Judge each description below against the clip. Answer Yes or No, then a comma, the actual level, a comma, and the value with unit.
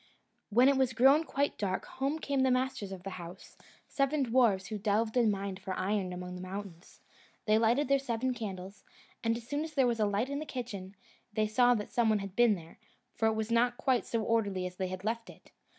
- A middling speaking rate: No, fast, 230 wpm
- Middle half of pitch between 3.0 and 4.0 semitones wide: No, average, 4.4 semitones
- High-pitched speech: Yes, high, 225 Hz